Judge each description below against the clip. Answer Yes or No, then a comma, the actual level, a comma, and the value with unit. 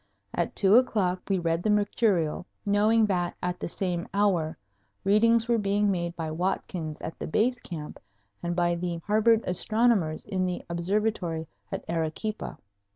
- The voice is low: No, medium, 185 Hz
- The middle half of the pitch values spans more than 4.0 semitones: No, average, 3.6 semitones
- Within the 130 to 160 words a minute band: Yes, average, 155 wpm